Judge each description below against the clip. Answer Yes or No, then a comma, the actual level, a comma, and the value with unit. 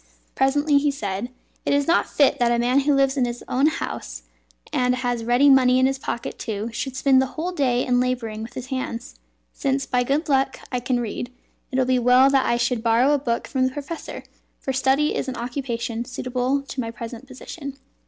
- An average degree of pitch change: No, narrow, 2.2 semitones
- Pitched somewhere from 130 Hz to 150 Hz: No, very high, 255 Hz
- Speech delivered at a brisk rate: Yes, fast, 210 wpm